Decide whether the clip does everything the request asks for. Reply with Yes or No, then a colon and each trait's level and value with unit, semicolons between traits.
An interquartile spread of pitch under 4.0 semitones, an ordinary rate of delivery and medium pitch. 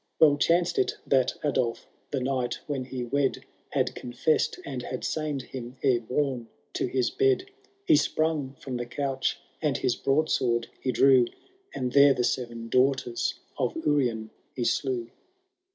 No: average, 2.7 semitones; average, 150 wpm; low, 130 Hz